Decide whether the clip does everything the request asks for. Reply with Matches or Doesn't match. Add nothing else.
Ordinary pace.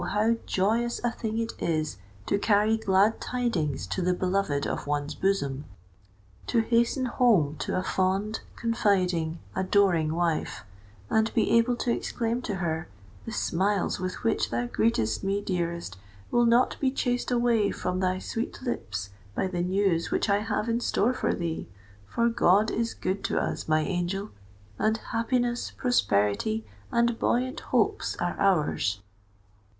Matches